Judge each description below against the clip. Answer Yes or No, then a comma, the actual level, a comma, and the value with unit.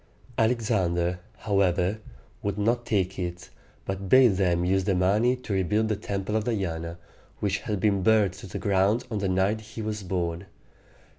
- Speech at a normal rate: Yes, average, 165 wpm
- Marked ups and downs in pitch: No, average, 2.8 semitones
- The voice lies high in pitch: No, low, 100 Hz